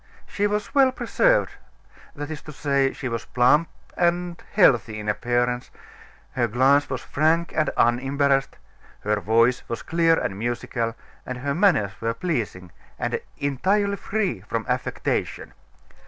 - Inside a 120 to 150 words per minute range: Yes, average, 140 wpm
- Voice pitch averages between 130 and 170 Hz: Yes, low, 135 Hz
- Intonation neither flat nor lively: No, wide, 6.3 semitones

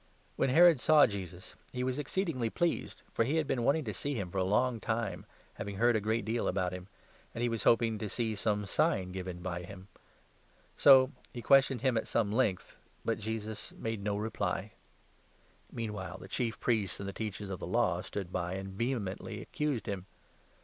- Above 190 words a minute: Yes, fast, 205 wpm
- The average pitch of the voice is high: No, low, 110 Hz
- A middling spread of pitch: Yes, average, 4.1 semitones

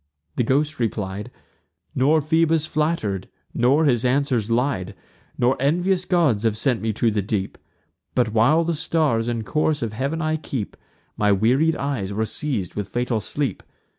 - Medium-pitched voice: No, low, 125 Hz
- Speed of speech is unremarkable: Yes, average, 160 wpm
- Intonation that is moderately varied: No, wide, 5.7 semitones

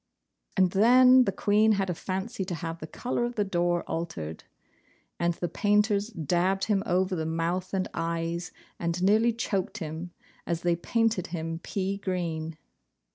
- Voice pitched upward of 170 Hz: Yes, medium, 185 Hz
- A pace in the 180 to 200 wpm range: No, average, 160 wpm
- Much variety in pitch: No, average, 3.5 semitones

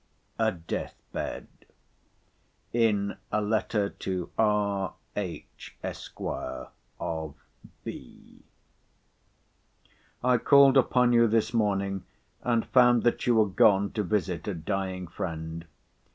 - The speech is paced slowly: Yes, slow, 105 wpm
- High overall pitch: No, low, 105 Hz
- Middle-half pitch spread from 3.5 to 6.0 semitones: Yes, average, 3.9 semitones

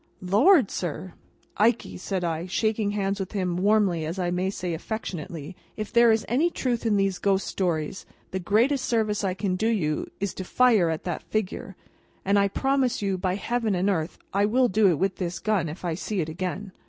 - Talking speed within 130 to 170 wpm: No, average, 200 wpm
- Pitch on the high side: Yes, high, 195 Hz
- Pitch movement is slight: No, average, 3.4 semitones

